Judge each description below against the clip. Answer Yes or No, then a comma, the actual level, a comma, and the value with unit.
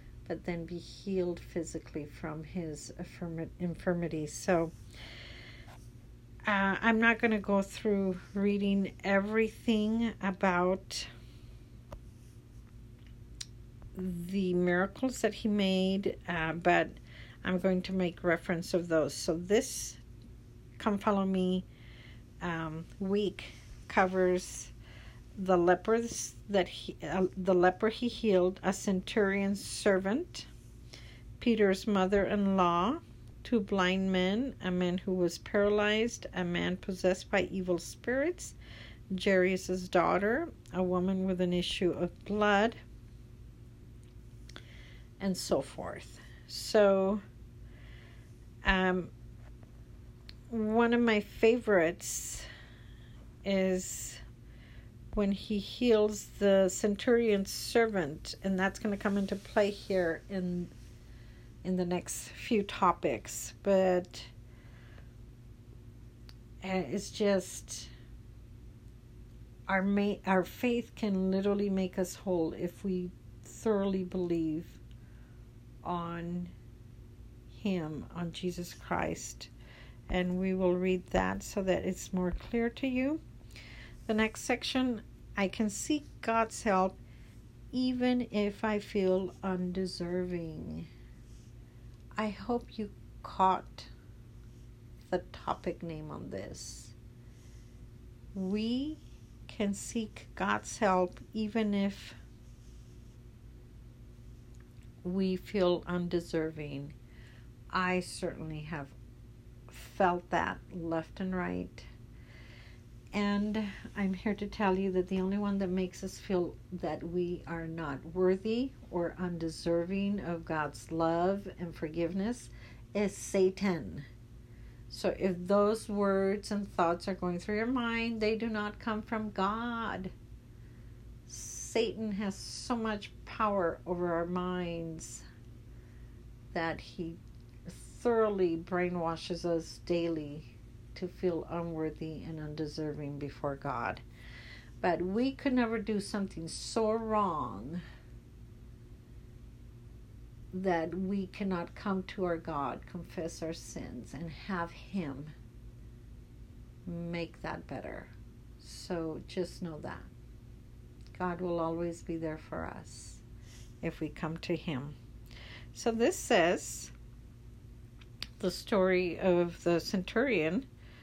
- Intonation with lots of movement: Yes, wide, 8.6 semitones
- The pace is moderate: No, slow, 105 wpm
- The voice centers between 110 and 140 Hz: No, medium, 175 Hz